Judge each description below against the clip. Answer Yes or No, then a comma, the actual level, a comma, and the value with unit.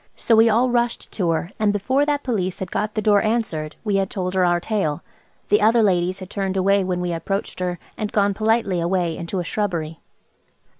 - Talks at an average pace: No, fast, 210 wpm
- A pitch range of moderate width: Yes, average, 3.4 semitones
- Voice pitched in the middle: No, high, 195 Hz